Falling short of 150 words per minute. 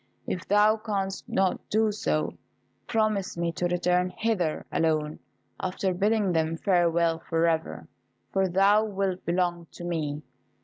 Yes: slow, 135 wpm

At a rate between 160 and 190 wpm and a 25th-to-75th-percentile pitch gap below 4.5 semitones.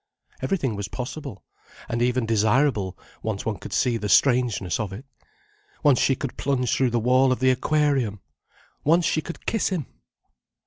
Yes: average, 165 wpm; average, 4.0 semitones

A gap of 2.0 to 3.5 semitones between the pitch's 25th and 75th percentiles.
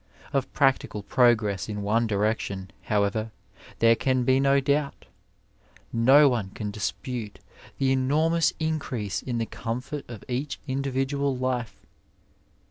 No: average, 4.0 semitones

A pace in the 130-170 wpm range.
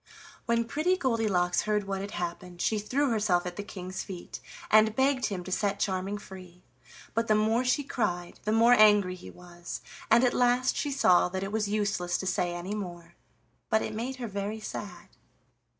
No: average, 190 wpm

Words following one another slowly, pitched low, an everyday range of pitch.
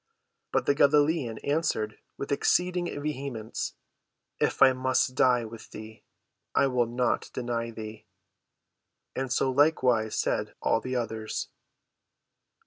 Yes: slow, 120 wpm; low, 125 Hz; average, 3.8 semitones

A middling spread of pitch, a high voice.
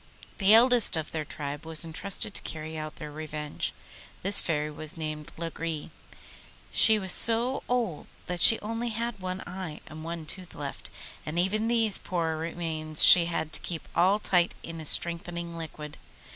No: average, 3.9 semitones; medium, 170 Hz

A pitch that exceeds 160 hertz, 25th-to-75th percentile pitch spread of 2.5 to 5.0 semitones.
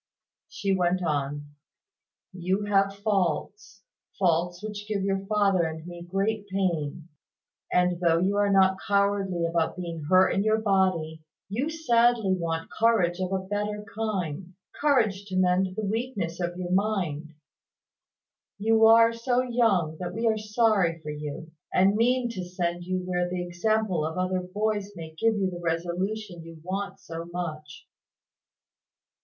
Yes: medium, 185 Hz; average, 3.3 semitones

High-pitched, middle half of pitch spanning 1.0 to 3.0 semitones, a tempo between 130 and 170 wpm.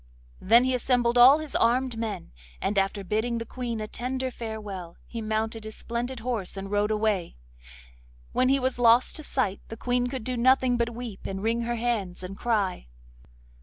No: high, 230 Hz; average, 2.7 semitones; average, 185 wpm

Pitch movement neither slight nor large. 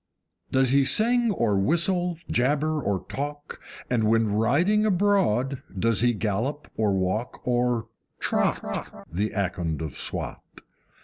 No: wide, 6.6 semitones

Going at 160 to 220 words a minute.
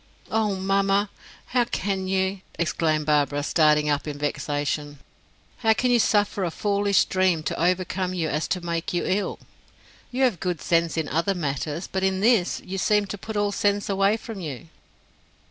Yes: average, 175 wpm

